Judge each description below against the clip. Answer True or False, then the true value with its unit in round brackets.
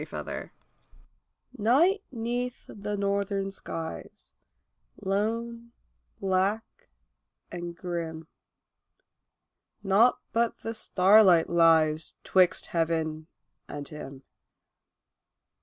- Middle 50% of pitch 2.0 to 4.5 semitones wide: False (5.3 semitones)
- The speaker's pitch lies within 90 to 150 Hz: False (195 Hz)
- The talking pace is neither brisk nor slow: False (75 wpm)